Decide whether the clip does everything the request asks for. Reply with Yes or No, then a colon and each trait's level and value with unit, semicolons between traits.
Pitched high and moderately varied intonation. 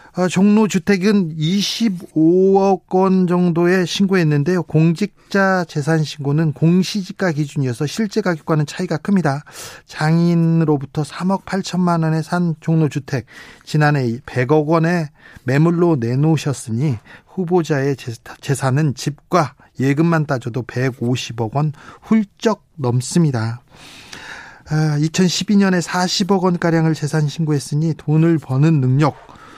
No: medium, 160 Hz; average, 3.9 semitones